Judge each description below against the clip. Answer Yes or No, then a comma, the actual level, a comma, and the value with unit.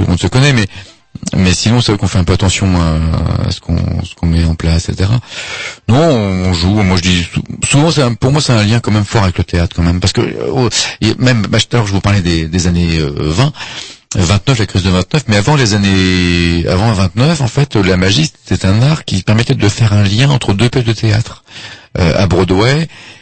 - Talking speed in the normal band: No, fast, 235 wpm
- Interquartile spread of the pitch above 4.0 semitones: Yes, average, 4.6 semitones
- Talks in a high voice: No, low, 100 Hz